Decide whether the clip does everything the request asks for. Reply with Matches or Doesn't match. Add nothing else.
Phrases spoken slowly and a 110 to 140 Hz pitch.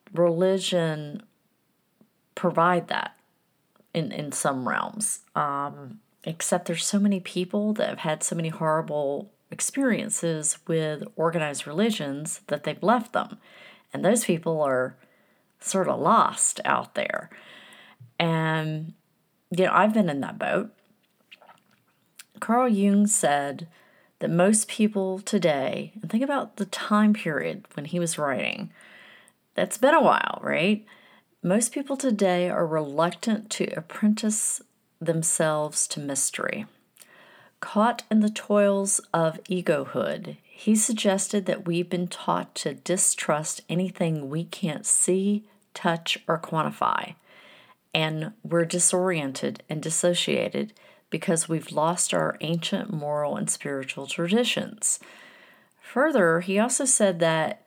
Doesn't match